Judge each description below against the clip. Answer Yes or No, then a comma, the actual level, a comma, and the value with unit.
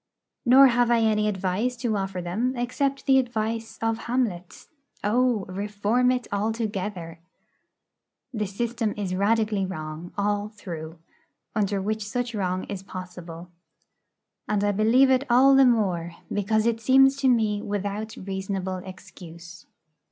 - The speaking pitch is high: Yes, high, 210 Hz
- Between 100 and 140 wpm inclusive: Yes, slow, 135 wpm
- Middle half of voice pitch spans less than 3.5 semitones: No, average, 4.0 semitones